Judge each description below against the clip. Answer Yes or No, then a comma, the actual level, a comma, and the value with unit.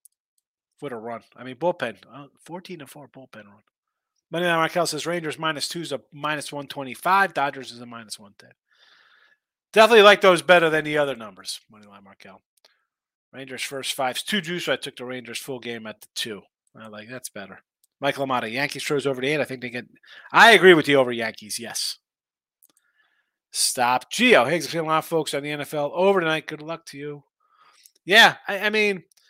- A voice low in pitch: No, medium, 145 Hz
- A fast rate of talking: No, average, 195 wpm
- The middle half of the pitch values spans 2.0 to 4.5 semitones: No, average, 5.2 semitones